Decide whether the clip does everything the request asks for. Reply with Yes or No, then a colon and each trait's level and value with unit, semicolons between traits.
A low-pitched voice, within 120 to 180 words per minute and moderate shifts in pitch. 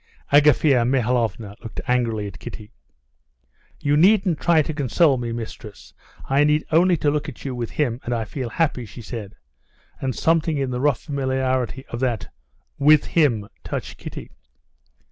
Yes: low, 130 Hz; average, 160 wpm; average, 4.2 semitones